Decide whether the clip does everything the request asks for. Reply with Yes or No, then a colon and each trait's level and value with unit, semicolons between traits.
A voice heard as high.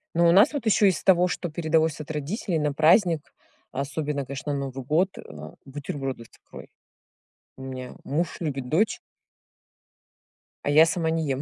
No: medium, 155 Hz